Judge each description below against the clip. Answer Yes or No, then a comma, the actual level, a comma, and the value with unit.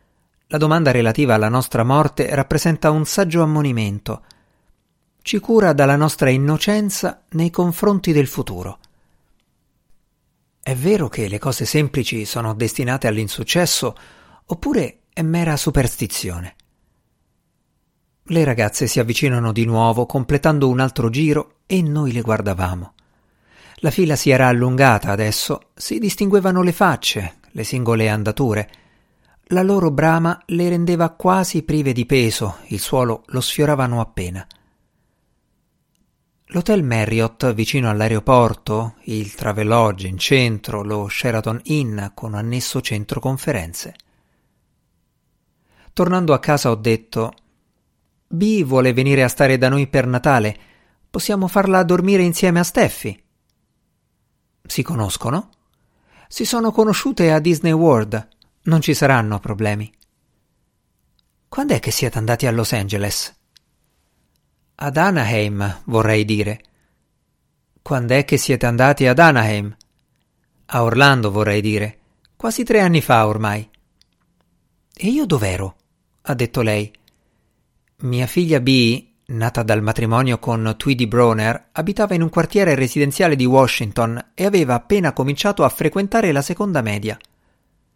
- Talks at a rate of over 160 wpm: No, average, 120 wpm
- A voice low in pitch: Yes, low, 130 Hz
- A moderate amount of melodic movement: No, wide, 6.4 semitones